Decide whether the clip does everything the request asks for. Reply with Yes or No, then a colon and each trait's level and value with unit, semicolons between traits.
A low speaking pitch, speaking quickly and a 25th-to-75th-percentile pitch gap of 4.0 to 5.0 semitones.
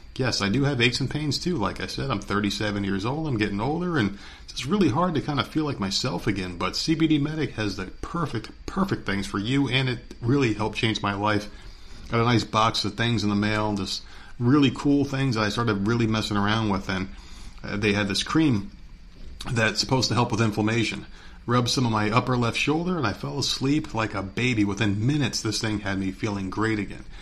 Yes: low, 110 Hz; fast, 225 wpm; average, 4.5 semitones